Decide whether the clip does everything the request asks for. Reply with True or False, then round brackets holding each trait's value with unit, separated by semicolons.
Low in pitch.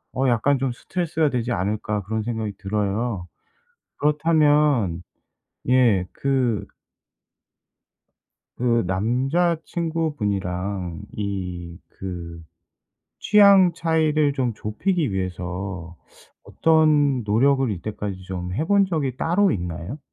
True (120 Hz)